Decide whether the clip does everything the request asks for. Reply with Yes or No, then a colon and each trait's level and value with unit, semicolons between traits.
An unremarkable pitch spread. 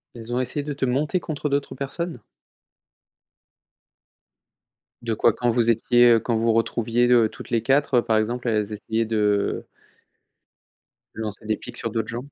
No: narrow, 2.3 semitones